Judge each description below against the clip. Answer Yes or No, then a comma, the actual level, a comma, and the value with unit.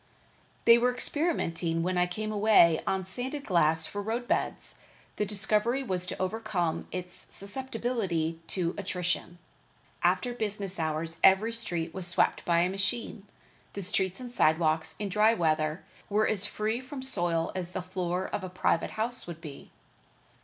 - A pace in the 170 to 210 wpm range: No, average, 155 wpm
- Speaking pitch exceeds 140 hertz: Yes, high, 190 Hz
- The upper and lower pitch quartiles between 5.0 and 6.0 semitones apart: No, average, 4.2 semitones